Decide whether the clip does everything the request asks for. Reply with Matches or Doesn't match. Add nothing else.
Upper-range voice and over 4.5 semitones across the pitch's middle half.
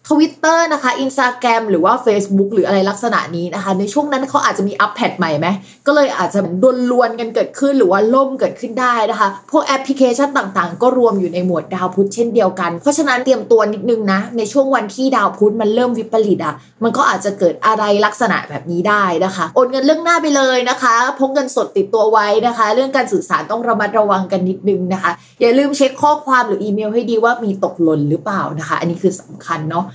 Matches